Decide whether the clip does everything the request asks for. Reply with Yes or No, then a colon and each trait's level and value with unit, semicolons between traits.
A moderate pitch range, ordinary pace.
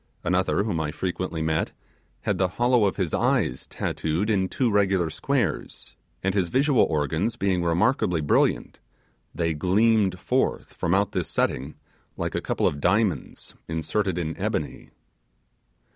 Yes: average, 4.2 semitones; average, 145 wpm